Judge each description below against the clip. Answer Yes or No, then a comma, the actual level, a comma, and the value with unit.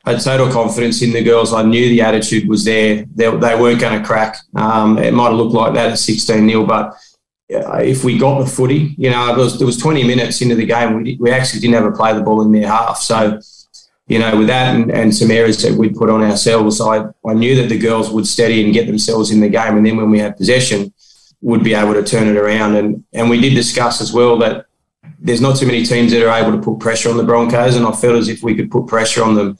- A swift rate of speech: Yes, fast, 270 wpm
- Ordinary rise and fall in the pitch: No, narrow, 1.7 semitones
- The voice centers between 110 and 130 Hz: Yes, low, 115 Hz